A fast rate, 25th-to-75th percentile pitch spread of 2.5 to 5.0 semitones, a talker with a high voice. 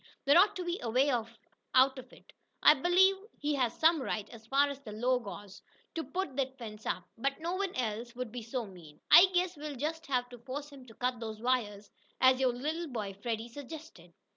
Yes: fast, 215 wpm; average, 4.6 semitones; very high, 255 Hz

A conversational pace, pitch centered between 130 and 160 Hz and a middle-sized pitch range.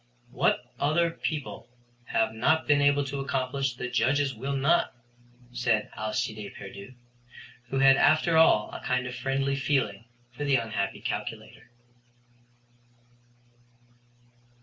No: slow, 125 wpm; low, 135 Hz; average, 3.3 semitones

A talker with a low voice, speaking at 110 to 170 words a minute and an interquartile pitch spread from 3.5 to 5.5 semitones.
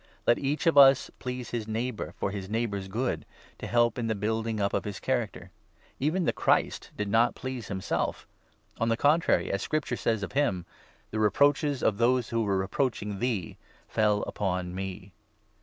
No: low, 115 Hz; average, 190 wpm; average, 4.1 semitones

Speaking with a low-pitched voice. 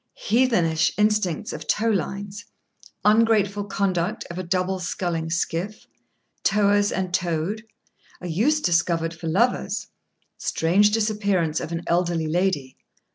No: medium, 185 Hz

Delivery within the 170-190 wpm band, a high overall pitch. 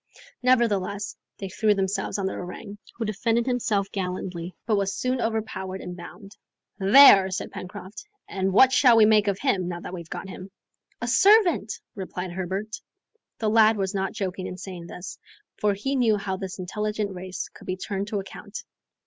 Yes: average, 175 wpm; high, 200 Hz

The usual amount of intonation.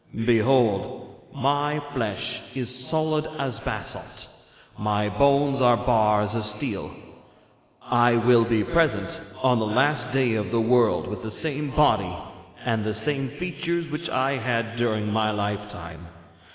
Yes: average, 4.4 semitones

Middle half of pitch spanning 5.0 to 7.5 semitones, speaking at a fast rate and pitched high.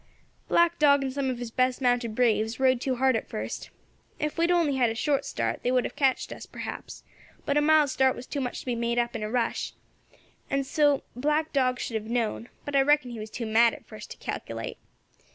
No: average, 3.2 semitones; fast, 235 wpm; very high, 255 Hz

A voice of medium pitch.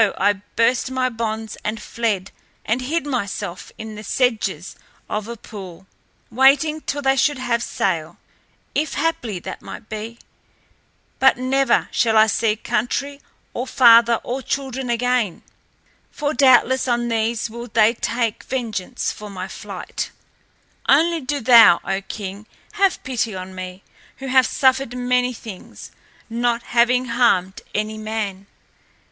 No: high, 235 Hz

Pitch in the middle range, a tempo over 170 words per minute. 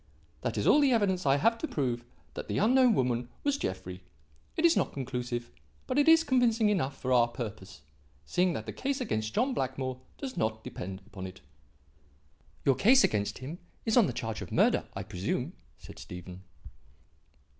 No: low, 130 Hz; average, 180 wpm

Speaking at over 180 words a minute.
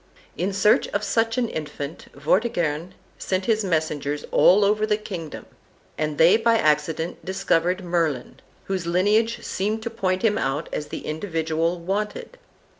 No: average, 145 wpm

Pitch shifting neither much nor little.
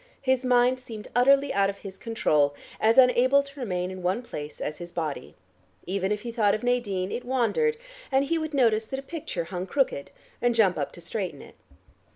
No: wide, 5.9 semitones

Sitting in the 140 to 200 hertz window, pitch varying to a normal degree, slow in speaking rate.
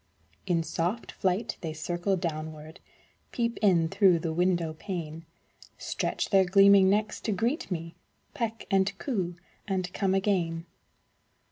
Yes: medium, 185 Hz; average, 3.2 semitones; slow, 130 wpm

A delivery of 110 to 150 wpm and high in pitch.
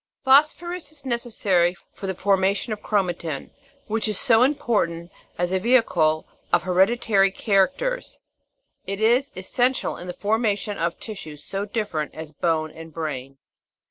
Yes: average, 140 wpm; high, 195 Hz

